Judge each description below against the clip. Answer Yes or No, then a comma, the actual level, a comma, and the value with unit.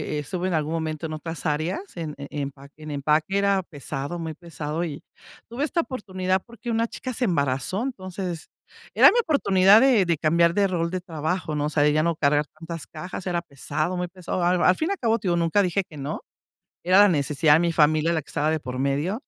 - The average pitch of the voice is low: No, medium, 170 Hz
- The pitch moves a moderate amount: Yes, average, 3.9 semitones